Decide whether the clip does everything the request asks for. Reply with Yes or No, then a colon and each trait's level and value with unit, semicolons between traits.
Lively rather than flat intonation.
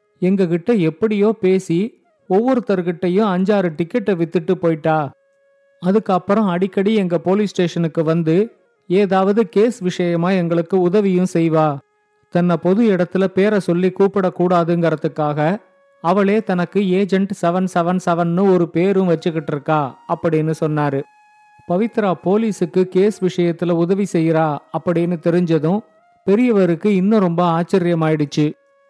No: average, 3.1 semitones